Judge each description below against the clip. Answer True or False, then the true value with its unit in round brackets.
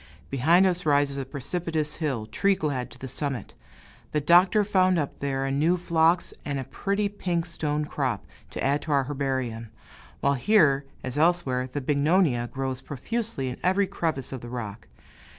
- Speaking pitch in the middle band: True (145 Hz)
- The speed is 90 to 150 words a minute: False (170 wpm)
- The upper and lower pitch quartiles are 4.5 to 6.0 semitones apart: True (4.8 semitones)